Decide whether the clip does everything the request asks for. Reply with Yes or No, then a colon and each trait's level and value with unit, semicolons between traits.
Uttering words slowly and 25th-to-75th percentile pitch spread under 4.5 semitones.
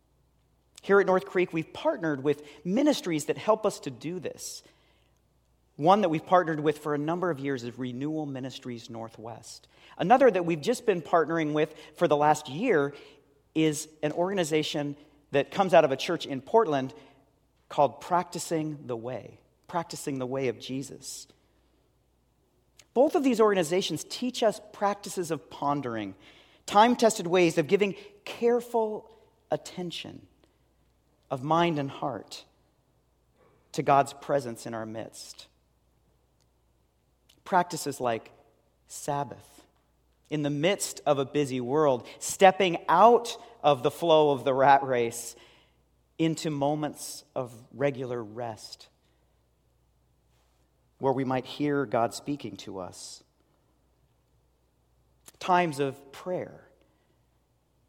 No: slow, 125 wpm; wide, 5.4 semitones